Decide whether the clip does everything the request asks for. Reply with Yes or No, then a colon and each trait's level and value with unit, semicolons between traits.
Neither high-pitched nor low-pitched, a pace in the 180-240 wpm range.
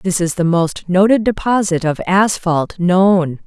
No: medium, 180 Hz; average, 155 wpm